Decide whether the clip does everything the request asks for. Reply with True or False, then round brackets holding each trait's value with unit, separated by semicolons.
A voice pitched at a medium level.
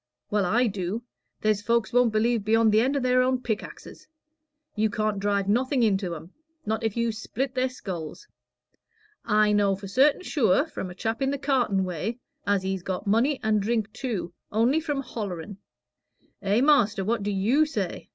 False (220 Hz)